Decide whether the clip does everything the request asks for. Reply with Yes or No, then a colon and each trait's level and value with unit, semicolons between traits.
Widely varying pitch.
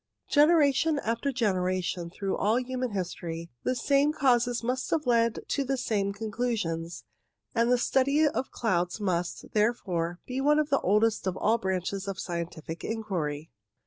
Yes: wide, 6.0 semitones